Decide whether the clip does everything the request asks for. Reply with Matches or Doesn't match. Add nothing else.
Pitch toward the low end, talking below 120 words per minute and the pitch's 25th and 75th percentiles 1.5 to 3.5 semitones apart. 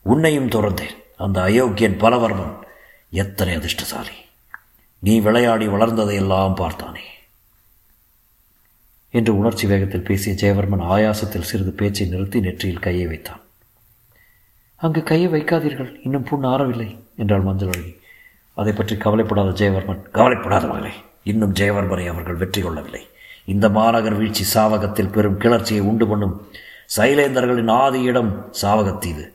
Matches